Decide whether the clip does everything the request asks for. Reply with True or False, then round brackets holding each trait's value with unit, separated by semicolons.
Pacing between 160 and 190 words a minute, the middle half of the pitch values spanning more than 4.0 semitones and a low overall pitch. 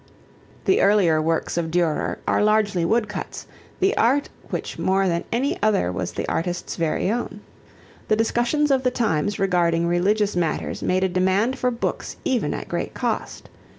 False (165 wpm; 5.1 semitones; 200 Hz)